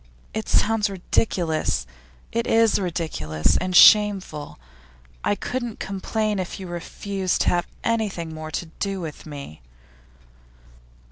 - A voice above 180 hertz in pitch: Yes, high, 190 Hz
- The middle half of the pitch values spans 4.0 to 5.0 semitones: Yes, average, 4.5 semitones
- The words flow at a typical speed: No, slow, 120 wpm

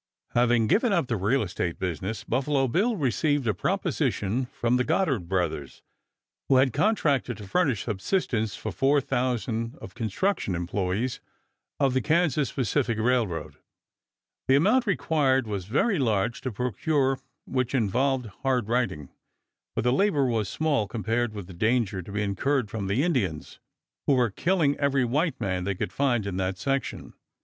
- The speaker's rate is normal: Yes, average, 155 wpm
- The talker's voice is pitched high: No, low, 125 Hz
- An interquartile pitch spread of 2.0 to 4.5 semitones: No, average, 5.1 semitones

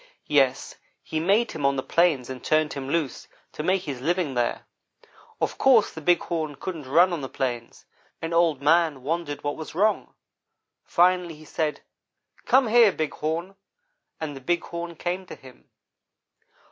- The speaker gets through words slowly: No, average, 170 wpm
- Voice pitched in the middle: Yes, medium, 160 Hz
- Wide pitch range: No, average, 3.7 semitones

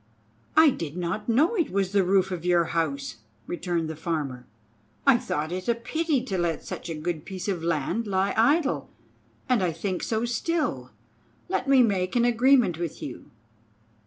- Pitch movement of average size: No, wide, 6.1 semitones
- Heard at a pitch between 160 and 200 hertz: Yes, high, 190 Hz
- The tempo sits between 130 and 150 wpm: No, average, 175 wpm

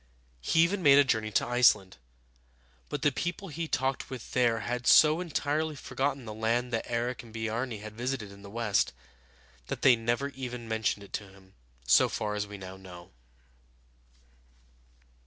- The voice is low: Yes, low, 120 Hz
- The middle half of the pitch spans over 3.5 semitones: Yes, average, 4.2 semitones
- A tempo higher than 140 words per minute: Yes, average, 170 wpm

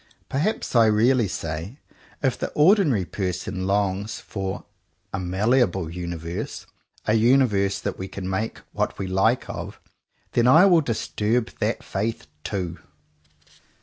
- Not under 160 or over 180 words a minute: No, average, 140 wpm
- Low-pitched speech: Yes, low, 100 Hz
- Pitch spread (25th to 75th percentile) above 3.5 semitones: Yes, average, 4.5 semitones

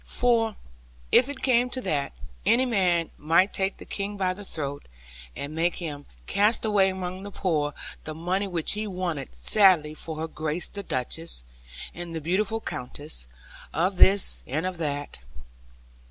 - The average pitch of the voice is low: No, medium, 180 Hz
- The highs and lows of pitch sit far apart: No, average, 4.5 semitones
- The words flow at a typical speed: Yes, average, 160 wpm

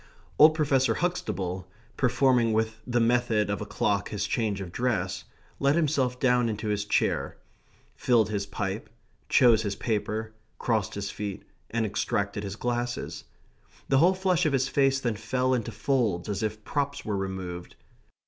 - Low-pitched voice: Yes, low, 110 Hz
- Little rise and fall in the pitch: No, average, 4.1 semitones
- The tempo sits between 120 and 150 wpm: No, average, 160 wpm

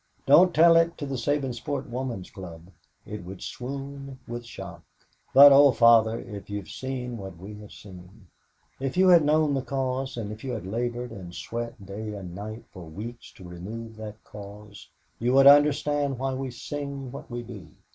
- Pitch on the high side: No, low, 120 Hz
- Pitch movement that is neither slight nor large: Yes, average, 5.0 semitones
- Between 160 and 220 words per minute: Yes, average, 180 wpm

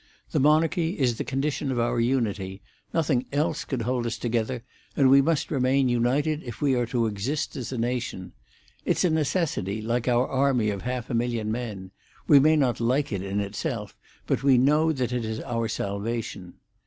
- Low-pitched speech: Yes, low, 125 Hz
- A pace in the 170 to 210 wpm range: Yes, average, 190 wpm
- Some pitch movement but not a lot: Yes, average, 3.6 semitones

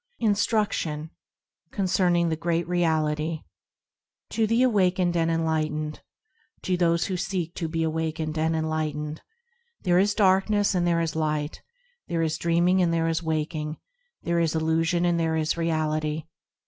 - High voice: No, medium, 165 Hz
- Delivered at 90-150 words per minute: Yes, average, 145 wpm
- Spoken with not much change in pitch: Yes, narrow, 2.0 semitones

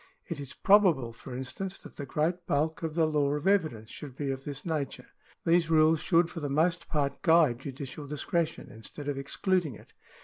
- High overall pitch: No, medium, 150 Hz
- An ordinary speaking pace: Yes, average, 195 wpm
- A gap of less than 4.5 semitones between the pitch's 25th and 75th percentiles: Yes, average, 3.1 semitones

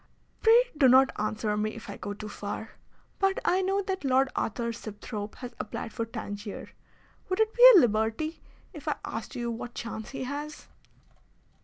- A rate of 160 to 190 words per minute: Yes, average, 175 wpm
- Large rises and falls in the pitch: Yes, wide, 6.2 semitones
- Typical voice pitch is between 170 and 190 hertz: No, high, 240 Hz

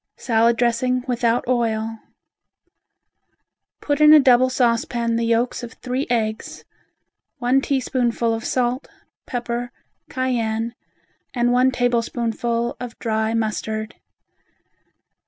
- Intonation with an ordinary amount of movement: No, narrow, 1.6 semitones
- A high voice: Yes, high, 240 Hz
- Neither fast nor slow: No, slow, 100 wpm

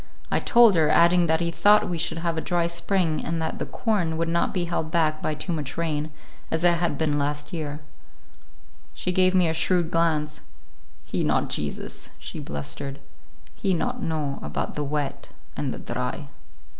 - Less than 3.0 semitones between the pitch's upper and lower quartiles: Yes, narrow, 2.5 semitones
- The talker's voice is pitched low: No, medium, 165 Hz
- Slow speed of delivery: No, average, 185 wpm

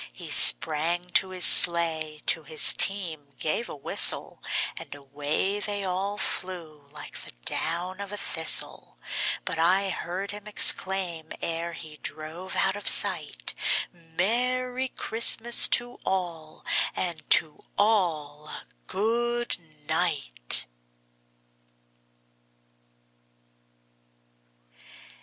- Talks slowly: Yes, slow, 100 wpm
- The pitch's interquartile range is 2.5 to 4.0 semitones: No, average, 4.4 semitones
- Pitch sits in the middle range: Yes, medium, 175 Hz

